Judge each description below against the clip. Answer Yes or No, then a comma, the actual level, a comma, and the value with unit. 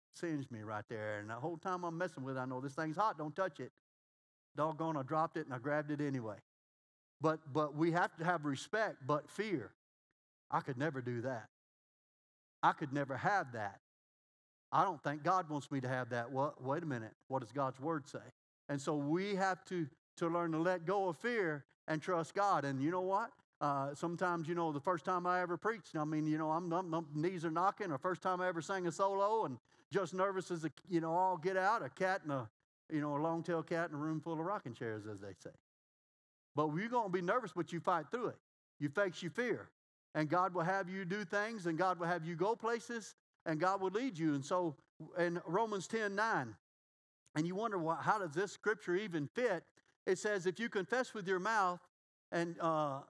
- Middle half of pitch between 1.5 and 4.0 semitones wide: No, average, 4.4 semitones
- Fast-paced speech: Yes, fast, 230 wpm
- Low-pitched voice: No, medium, 165 Hz